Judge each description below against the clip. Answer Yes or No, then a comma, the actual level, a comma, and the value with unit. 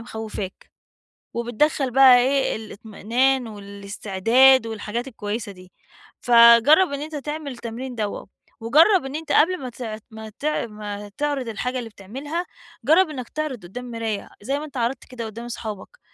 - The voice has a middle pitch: No, high, 240 Hz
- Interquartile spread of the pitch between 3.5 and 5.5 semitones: Yes, average, 4.0 semitones